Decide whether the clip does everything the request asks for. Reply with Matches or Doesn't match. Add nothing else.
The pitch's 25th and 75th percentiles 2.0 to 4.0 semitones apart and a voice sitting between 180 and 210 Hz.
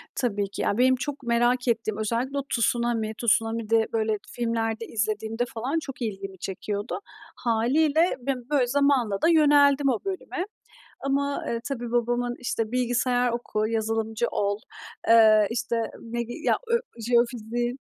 Doesn't match